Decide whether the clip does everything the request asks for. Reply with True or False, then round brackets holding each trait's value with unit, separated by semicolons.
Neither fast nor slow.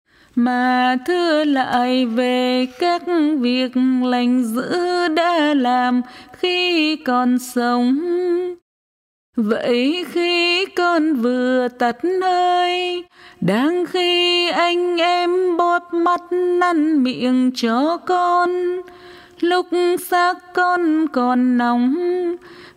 False (90 wpm)